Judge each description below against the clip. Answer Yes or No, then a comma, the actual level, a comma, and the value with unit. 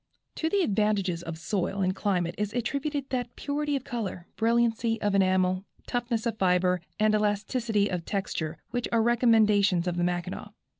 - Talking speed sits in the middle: Yes, average, 160 wpm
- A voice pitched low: No, high, 210 Hz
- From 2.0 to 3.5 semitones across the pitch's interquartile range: No, average, 4.3 semitones